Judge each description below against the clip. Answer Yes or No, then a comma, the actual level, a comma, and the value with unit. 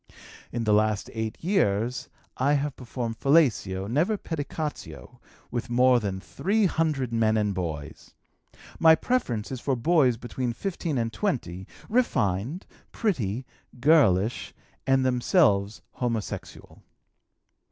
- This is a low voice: Yes, low, 125 Hz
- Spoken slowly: Yes, slow, 115 wpm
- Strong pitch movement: Yes, wide, 6.0 semitones